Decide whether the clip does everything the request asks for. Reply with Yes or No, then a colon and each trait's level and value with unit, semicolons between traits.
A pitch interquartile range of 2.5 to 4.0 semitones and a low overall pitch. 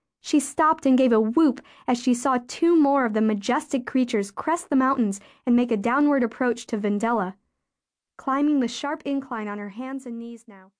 No: average, 3.7 semitones; very high, 250 Hz